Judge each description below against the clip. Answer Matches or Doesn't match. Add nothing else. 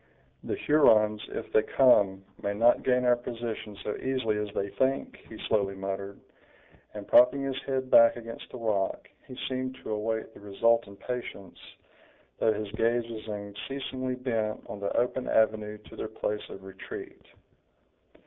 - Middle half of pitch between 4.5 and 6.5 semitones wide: Doesn't match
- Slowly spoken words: Doesn't match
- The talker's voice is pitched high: Doesn't match